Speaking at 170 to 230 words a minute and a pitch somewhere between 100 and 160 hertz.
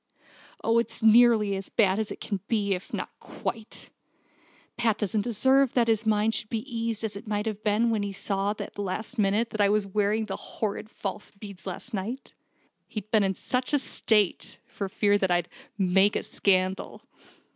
No: average, 190 wpm; high, 210 Hz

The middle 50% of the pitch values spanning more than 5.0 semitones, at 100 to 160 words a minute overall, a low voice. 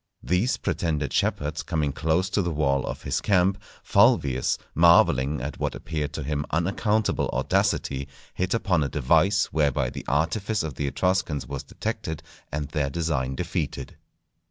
No: average, 4.2 semitones; average, 150 wpm; very low, 80 Hz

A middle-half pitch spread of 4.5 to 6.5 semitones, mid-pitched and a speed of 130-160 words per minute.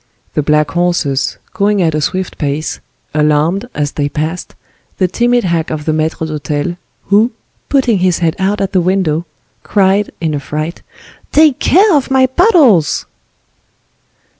Yes: average, 5.2 semitones; medium, 175 Hz; average, 150 wpm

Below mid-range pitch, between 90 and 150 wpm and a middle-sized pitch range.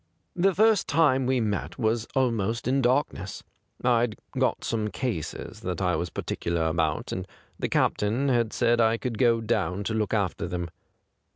No: low, 115 Hz; average, 170 wpm; average, 4.9 semitones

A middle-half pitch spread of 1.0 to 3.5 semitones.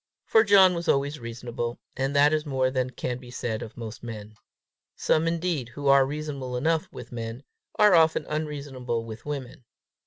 No: average, 4.1 semitones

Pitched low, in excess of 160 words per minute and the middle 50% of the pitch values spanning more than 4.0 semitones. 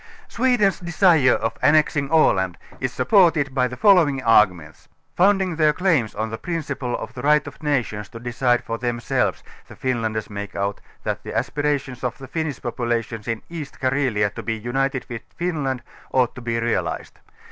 Yes: low, 130 Hz; average, 170 wpm; average, 4.9 semitones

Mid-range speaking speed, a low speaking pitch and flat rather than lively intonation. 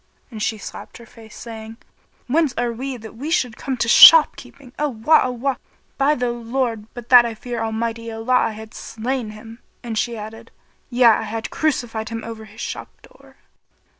No: average, 180 wpm; high, 230 Hz; narrow, 2.1 semitones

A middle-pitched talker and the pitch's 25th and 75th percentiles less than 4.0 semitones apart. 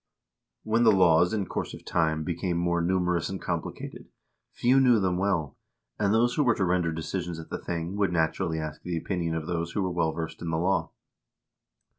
No: very low, 90 Hz; average, 2.9 semitones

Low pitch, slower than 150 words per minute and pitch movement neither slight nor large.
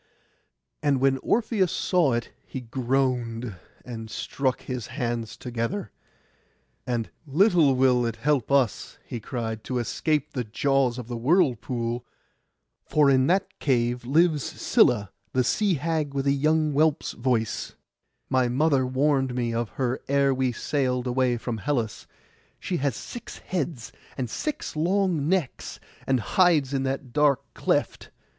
Yes: low, 130 Hz; average, 140 wpm; average, 3.7 semitones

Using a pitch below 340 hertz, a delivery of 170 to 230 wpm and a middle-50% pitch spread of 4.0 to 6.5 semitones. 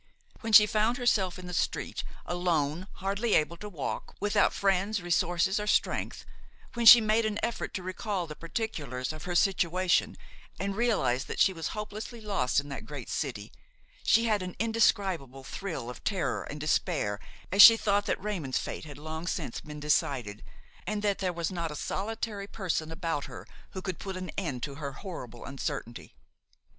Yes: medium, 185 Hz; average, 175 wpm; average, 5.3 semitones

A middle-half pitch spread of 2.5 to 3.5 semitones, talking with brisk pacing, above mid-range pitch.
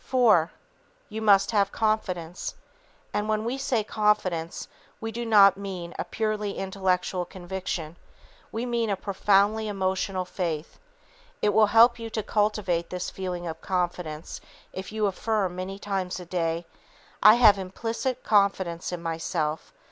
No: average, 3.2 semitones; average, 145 wpm; high, 195 Hz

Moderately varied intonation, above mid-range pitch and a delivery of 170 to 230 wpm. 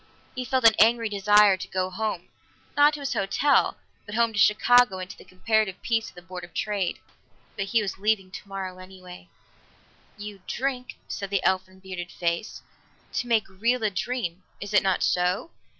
Yes: average, 3.4 semitones; high, 200 Hz; average, 180 wpm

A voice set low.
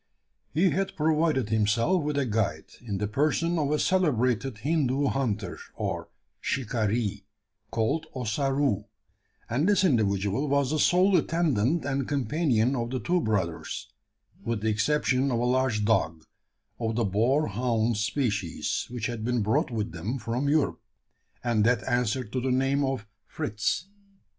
Yes: low, 125 Hz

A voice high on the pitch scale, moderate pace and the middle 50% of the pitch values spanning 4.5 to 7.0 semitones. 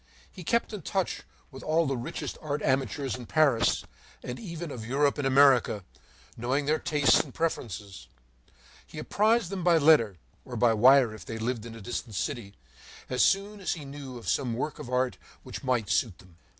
No: low, 135 Hz; average, 190 wpm; average, 4.9 semitones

